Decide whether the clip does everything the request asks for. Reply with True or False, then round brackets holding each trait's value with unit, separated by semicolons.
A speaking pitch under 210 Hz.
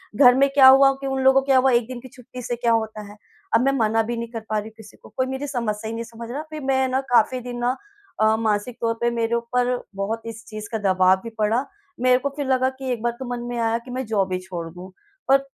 False (235 Hz)